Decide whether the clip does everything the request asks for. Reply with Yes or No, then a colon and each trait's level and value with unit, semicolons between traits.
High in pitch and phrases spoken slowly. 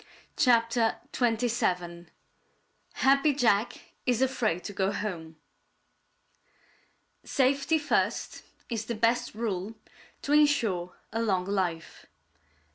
Yes: high, 225 Hz; slow, 95 wpm